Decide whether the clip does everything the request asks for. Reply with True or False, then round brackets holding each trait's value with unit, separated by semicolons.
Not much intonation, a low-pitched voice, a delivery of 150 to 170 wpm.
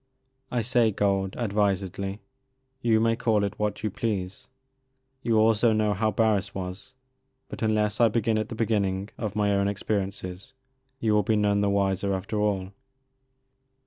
True (2.2 semitones; 105 Hz; 160 wpm)